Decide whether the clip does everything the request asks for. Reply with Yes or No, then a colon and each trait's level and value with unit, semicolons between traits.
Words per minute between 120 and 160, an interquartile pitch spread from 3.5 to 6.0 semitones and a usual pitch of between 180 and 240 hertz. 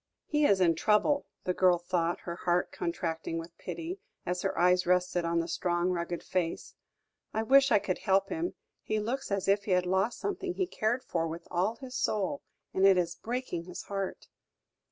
No: average, 195 wpm; average, 4.2 semitones; medium, 185 Hz